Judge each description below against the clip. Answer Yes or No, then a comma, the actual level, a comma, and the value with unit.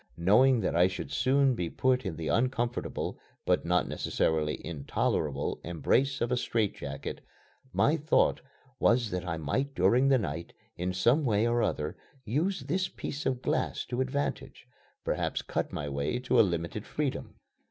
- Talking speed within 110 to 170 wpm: Yes, average, 165 wpm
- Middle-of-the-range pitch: No, low, 115 Hz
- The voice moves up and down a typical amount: No, wide, 7.5 semitones